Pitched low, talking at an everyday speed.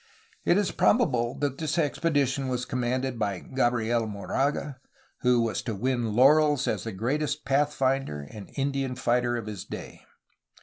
Yes: low, 130 Hz; average, 145 wpm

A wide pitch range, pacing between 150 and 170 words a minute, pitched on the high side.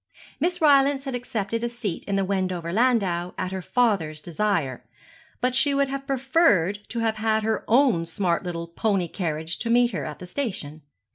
No: wide, 6.1 semitones; average, 185 wpm; high, 210 Hz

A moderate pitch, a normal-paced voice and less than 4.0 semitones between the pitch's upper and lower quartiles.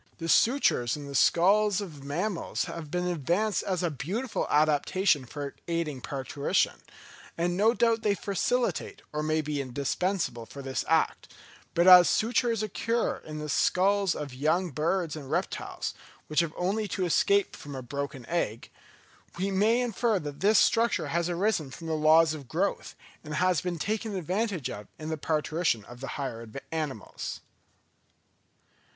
No: medium, 165 Hz; average, 160 wpm; wide, 5.4 semitones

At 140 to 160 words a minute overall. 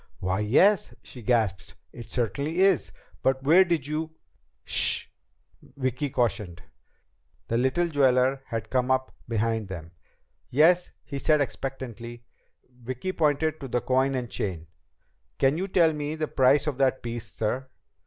Yes: average, 155 wpm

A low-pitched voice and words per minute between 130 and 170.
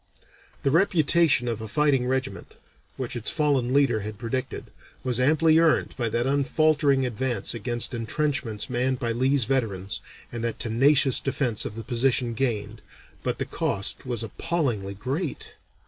Yes: low, 125 Hz; average, 145 wpm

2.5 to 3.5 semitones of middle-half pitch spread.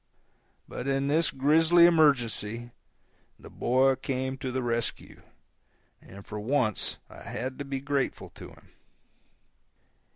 Yes: average, 3.0 semitones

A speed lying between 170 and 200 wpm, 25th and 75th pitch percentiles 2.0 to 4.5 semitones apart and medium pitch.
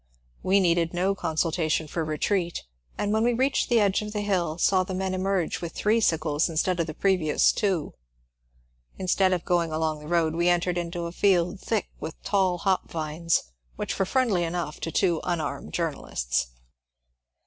Yes: average, 180 wpm; average, 2.8 semitones; medium, 175 Hz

